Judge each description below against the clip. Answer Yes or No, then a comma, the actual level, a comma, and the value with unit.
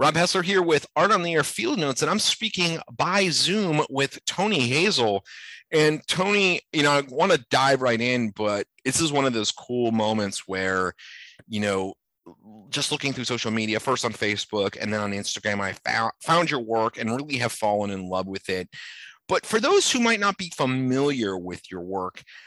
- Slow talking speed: No, average, 200 wpm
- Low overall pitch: Yes, low, 120 Hz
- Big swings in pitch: Yes, wide, 6.7 semitones